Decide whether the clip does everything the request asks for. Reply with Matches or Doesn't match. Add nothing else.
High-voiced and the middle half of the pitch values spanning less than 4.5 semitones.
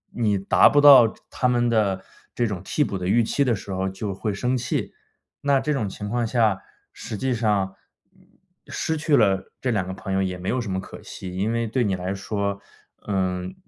Doesn't match